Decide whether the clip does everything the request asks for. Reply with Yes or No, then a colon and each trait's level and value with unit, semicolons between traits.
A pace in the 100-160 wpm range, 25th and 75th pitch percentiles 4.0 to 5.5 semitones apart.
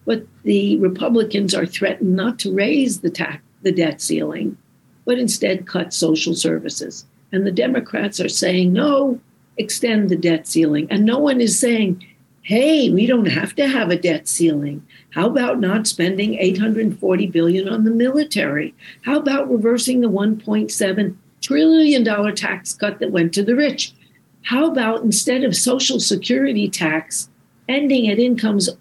Yes: average, 155 wpm; average, 5.2 semitones